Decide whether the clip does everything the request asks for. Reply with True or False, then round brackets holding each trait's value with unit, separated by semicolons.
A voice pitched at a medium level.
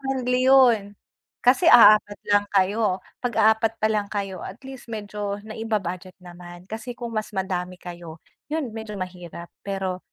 False (205 Hz)